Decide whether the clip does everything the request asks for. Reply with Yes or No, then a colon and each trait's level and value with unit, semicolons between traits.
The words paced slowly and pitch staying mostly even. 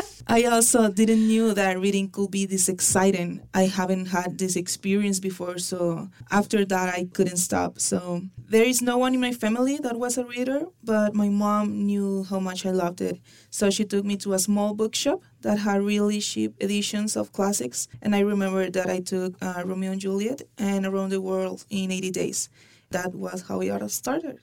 No: average, 200 wpm; narrow, 2.2 semitones